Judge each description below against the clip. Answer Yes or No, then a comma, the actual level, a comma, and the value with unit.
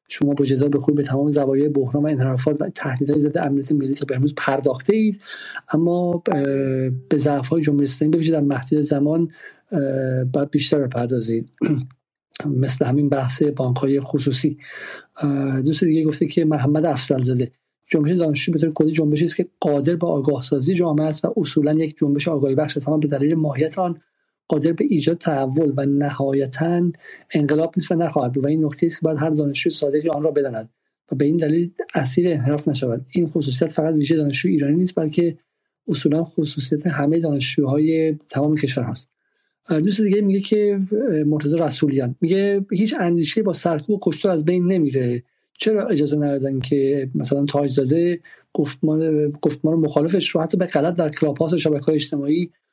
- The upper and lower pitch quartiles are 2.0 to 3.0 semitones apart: Yes, narrow, 2.6 semitones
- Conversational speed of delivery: No, fast, 170 wpm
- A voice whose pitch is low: No, medium, 150 Hz